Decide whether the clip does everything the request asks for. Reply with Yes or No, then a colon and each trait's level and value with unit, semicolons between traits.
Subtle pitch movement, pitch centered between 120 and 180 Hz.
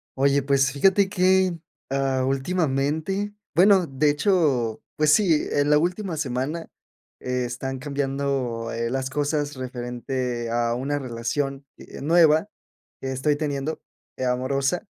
No: average, 3.4 semitones; medium, 140 Hz